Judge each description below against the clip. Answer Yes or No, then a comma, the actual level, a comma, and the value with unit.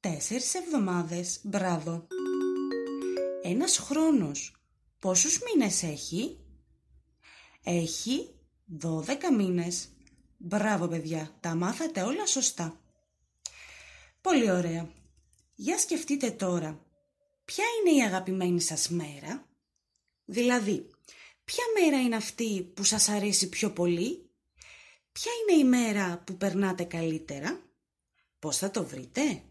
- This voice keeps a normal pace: No, slow, 100 wpm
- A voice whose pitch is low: No, high, 190 Hz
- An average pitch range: No, wide, 8.3 semitones